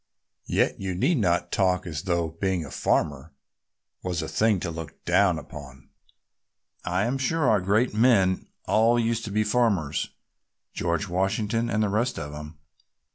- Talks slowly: No, average, 160 wpm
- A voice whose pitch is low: Yes, very low, 95 Hz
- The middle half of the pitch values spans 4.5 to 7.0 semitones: Yes, average, 4.9 semitones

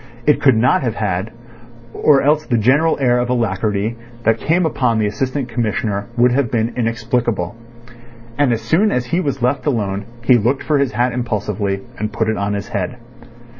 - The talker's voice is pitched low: Yes, low, 120 Hz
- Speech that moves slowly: No, average, 180 wpm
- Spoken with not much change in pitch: No, average, 3.6 semitones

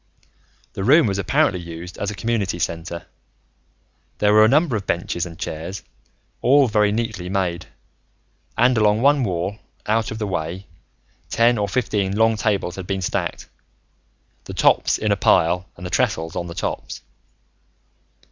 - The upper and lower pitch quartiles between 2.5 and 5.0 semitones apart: Yes, average, 3.9 semitones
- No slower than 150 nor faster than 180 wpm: Yes, average, 155 wpm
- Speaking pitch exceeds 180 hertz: No, low, 100 Hz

